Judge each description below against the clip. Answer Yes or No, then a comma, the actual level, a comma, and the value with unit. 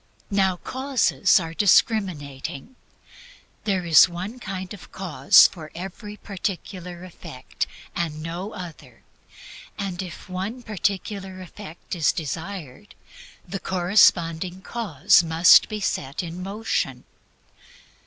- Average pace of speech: No, slow, 105 wpm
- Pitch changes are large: No, average, 3.2 semitones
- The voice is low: No, medium, 185 Hz